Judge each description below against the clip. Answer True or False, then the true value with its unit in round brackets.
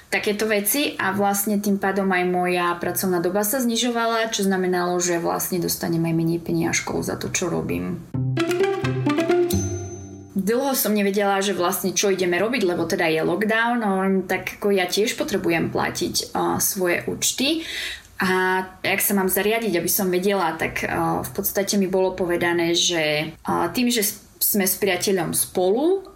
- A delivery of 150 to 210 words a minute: True (160 wpm)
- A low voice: False (190 Hz)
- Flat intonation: False (3.1 semitones)